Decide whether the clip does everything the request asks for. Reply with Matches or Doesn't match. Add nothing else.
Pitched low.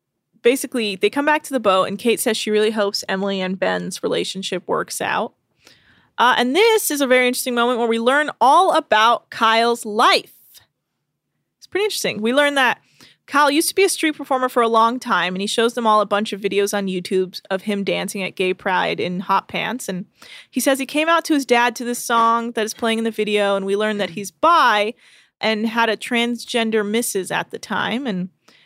Doesn't match